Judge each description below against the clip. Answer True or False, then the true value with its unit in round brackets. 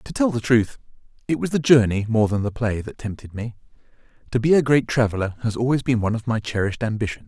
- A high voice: False (115 Hz)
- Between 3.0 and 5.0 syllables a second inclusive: False (6.5 syllables/s)